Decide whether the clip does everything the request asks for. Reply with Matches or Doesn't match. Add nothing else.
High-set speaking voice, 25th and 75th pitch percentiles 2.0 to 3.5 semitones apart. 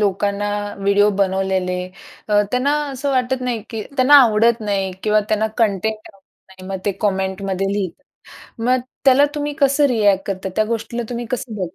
Doesn't match